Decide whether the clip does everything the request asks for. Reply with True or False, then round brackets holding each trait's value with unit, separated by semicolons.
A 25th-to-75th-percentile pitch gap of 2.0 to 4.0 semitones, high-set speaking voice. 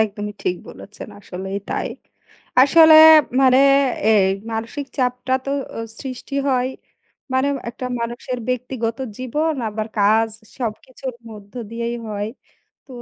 True (3.4 semitones; 240 Hz)